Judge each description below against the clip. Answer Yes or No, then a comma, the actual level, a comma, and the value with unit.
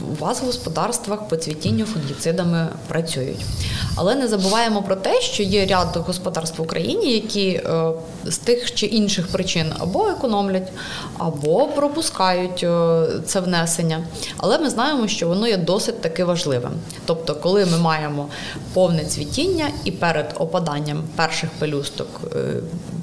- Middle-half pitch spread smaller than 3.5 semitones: No, average, 3.8 semitones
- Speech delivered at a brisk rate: No, average, 135 wpm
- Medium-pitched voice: Yes, medium, 170 Hz